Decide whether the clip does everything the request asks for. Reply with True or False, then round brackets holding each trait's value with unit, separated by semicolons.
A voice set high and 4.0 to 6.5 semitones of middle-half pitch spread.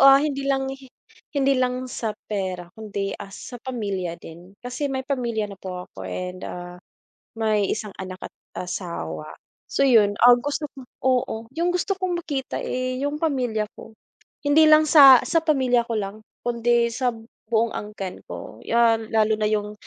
True (235 Hz; 5.1 semitones)